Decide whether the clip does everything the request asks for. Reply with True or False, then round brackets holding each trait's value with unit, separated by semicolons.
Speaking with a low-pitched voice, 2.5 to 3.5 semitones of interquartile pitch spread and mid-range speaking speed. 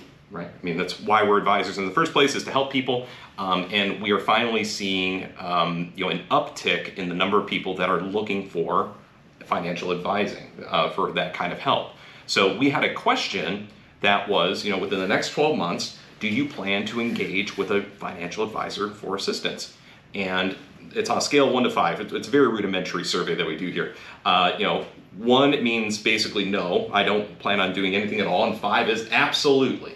False (100 Hz; 3.0 semitones; 210 wpm)